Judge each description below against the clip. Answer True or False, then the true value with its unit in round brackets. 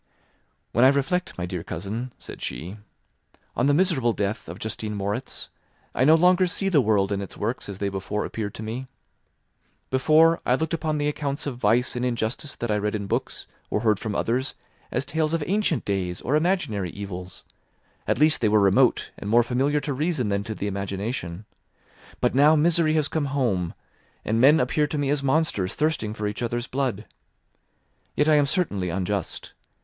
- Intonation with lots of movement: True (6.5 semitones)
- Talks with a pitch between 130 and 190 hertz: False (120 Hz)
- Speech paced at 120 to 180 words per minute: False (190 wpm)